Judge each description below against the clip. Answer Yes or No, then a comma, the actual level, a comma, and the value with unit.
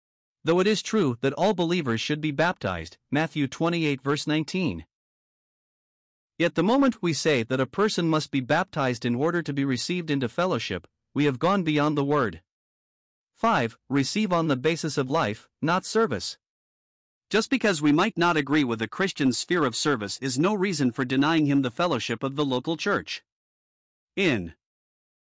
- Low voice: No, medium, 150 Hz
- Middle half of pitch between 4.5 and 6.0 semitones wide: Yes, average, 5.2 semitones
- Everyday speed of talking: Yes, average, 170 wpm